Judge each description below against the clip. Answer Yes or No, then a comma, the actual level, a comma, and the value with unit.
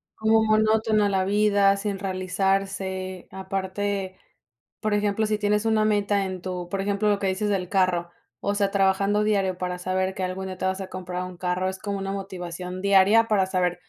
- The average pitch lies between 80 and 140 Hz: No, high, 195 Hz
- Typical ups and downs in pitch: No, narrow, 1.7 semitones